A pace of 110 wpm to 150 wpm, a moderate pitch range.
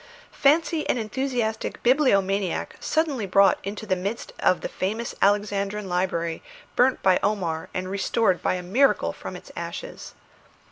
Yes: average, 140 wpm; average, 4.4 semitones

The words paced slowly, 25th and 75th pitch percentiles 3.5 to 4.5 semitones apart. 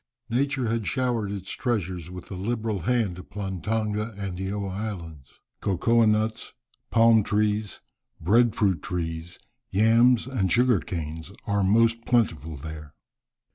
Yes: slow, 125 wpm; average, 4.1 semitones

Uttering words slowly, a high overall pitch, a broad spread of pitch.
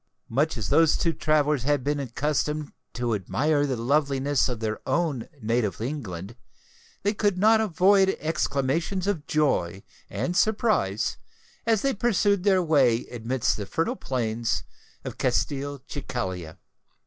No: slow, 130 wpm; medium, 145 Hz; wide, 6.4 semitones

